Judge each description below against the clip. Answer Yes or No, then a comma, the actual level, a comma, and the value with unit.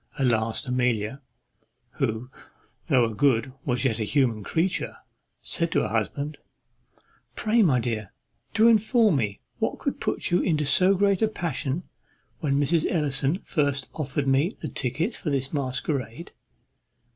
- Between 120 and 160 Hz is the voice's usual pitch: Yes, medium, 140 Hz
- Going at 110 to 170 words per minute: Yes, average, 145 wpm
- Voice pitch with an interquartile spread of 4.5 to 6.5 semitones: Yes, average, 5.2 semitones